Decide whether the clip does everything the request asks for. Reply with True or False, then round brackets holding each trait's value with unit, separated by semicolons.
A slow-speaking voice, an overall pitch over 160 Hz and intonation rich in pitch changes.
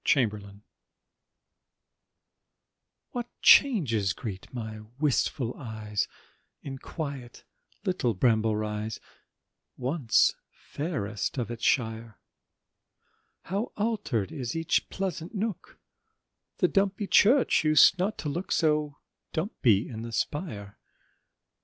False (100 wpm; 135 Hz; 7.9 semitones)